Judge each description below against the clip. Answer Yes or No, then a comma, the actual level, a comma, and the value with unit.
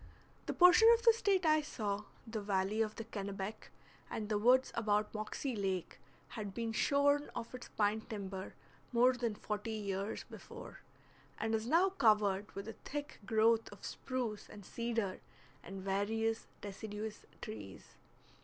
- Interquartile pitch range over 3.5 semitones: No, average, 3.1 semitones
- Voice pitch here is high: Yes, high, 220 Hz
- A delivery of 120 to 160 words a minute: Yes, average, 150 wpm